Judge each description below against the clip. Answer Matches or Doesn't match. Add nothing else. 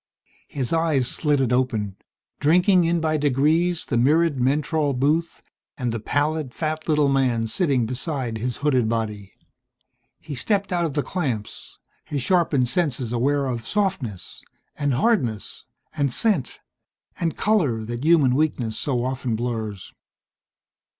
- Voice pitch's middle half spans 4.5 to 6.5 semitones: Matches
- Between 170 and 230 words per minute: Doesn't match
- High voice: Doesn't match